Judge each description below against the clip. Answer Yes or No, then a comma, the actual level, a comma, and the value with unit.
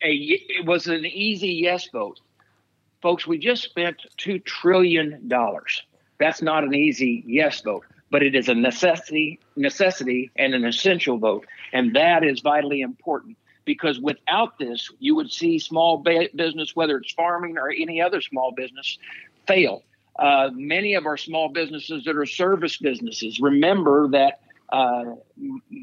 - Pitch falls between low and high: Yes, medium, 160 Hz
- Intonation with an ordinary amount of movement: Yes, average, 4.7 semitones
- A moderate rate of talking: Yes, average, 155 wpm